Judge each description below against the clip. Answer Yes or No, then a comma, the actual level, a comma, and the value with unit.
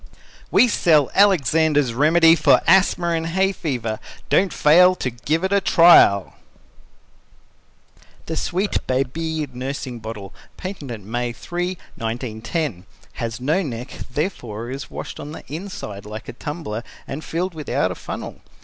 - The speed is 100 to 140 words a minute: Yes, slow, 135 wpm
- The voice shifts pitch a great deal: Yes, wide, 6.4 semitones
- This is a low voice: No, medium, 150 Hz